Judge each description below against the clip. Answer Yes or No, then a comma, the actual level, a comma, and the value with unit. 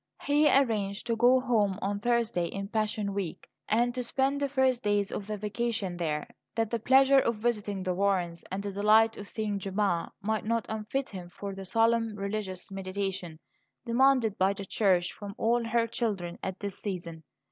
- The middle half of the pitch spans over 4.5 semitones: No, average, 3.2 semitones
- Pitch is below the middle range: No, high, 210 Hz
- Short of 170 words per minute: No, average, 180 wpm